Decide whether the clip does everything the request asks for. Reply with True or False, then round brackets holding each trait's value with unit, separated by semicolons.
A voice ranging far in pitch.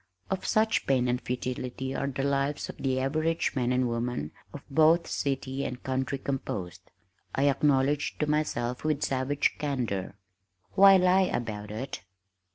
False (2.9 semitones)